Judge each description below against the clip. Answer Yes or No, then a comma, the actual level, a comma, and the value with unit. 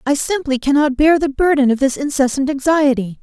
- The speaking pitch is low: No, very high, 280 Hz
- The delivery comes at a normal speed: Yes, average, 185 wpm